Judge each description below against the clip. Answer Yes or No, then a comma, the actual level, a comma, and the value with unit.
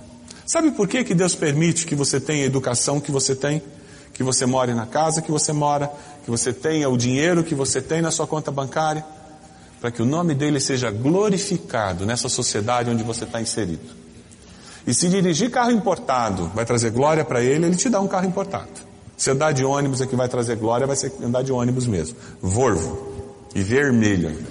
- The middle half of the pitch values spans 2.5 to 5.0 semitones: Yes, average, 4.4 semitones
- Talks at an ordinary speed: No, fast, 200 wpm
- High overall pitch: No, medium, 140 Hz